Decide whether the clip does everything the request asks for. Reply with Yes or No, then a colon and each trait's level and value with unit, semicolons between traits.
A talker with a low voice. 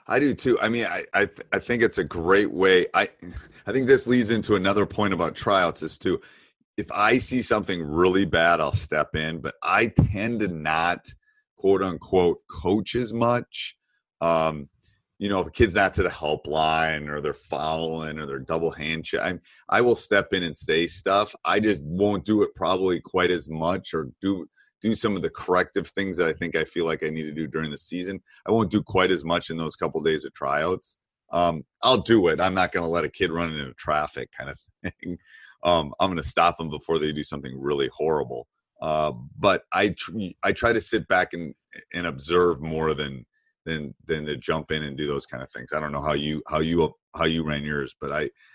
Yes: very low, 85 Hz